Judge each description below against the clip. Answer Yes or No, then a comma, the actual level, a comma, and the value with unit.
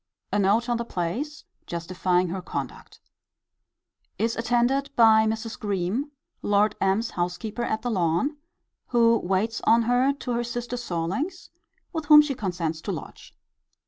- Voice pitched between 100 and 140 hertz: No, high, 225 Hz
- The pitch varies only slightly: No, average, 4.5 semitones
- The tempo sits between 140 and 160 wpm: Yes, average, 145 wpm